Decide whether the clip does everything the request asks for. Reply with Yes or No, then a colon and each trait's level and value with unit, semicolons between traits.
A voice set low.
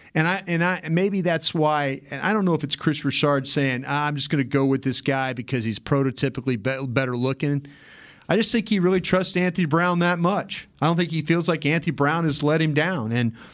No: medium, 150 Hz